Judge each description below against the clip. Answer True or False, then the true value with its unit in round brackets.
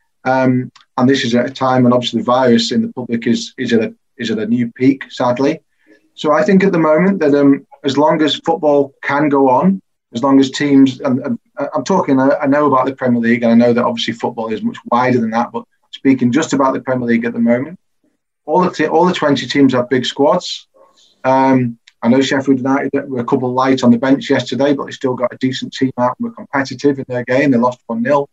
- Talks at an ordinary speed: False (245 wpm)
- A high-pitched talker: False (135 Hz)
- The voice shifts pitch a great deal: False (2.9 semitones)